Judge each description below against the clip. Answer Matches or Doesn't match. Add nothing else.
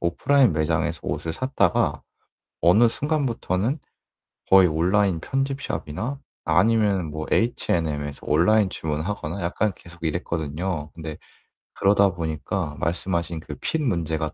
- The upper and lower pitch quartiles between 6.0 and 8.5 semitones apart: Doesn't match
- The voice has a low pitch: Matches